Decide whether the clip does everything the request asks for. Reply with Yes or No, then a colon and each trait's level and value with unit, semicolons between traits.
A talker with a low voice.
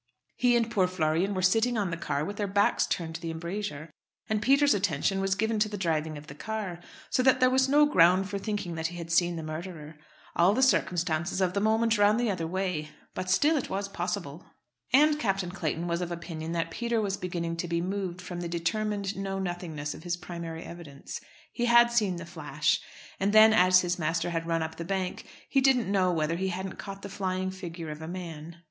No: medium, 185 Hz